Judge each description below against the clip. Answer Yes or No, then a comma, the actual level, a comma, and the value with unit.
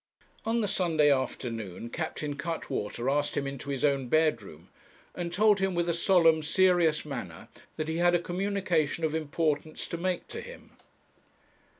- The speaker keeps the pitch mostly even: No, average, 3.9 semitones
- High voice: No, medium, 160 Hz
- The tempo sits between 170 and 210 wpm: No, average, 160 wpm